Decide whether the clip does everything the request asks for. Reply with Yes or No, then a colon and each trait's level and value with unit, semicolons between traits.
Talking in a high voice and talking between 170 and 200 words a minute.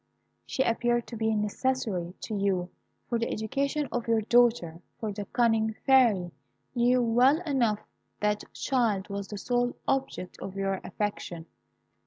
No: high, 225 Hz; average, 145 wpm